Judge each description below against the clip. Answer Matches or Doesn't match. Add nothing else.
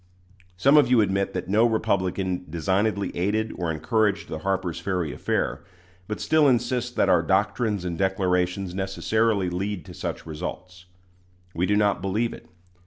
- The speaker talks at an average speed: Matches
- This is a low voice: Matches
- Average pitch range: Matches